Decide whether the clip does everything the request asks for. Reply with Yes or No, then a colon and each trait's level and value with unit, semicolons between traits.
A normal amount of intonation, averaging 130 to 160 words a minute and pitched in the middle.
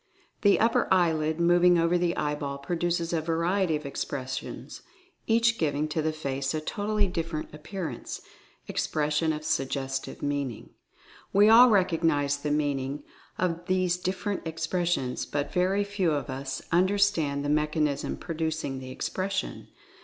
Yes: average, 3.9 semitones; average, 145 wpm; medium, 160 Hz